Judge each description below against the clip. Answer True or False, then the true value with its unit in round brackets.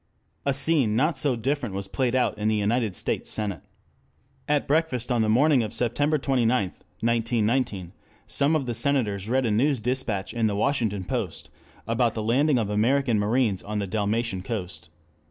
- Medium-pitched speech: False (115 Hz)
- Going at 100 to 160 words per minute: False (170 wpm)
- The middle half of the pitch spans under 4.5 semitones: True (4.0 semitones)